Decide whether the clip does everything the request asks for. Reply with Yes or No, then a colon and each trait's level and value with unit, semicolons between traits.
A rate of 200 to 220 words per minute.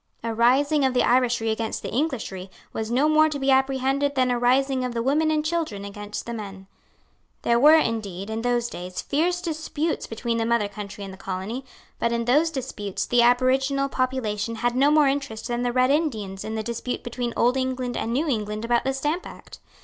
Yes: fast, 205 wpm